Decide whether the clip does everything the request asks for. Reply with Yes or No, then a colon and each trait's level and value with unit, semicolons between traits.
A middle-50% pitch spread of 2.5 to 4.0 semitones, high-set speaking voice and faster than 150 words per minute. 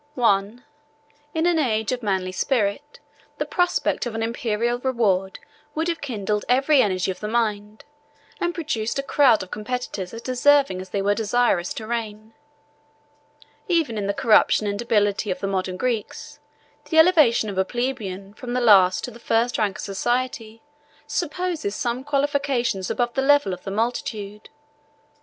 No: average, 4.4 semitones; high, 230 Hz; average, 160 wpm